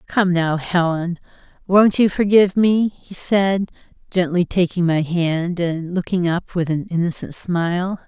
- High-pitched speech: No, medium, 180 Hz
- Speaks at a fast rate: No, average, 150 wpm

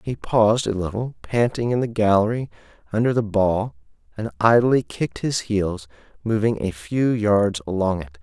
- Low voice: Yes, low, 105 Hz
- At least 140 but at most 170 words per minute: Yes, average, 160 wpm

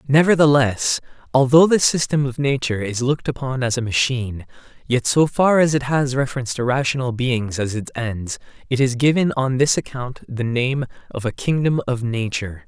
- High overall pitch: No, low, 130 Hz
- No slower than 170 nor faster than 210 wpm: Yes, average, 180 wpm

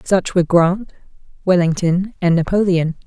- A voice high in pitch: No, medium, 180 Hz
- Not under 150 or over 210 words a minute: No, slow, 115 wpm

